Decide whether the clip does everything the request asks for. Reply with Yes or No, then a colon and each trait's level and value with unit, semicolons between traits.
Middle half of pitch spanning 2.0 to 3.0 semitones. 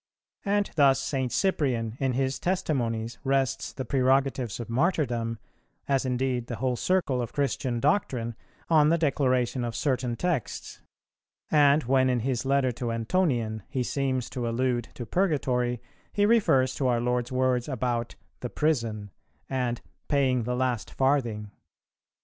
Yes: narrow, 2.6 semitones